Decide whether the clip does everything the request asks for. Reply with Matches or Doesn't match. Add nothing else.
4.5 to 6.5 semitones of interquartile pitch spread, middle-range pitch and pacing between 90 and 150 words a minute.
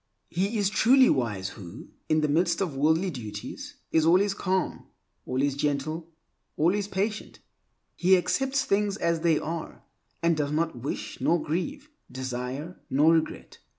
Matches